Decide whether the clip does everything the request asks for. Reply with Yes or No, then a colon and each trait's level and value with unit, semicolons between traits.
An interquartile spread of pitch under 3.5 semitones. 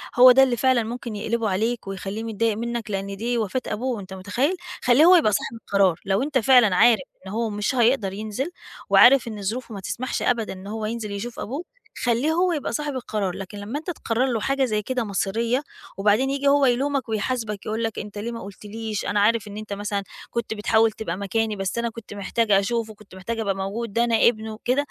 Yes: average, 3.0 semitones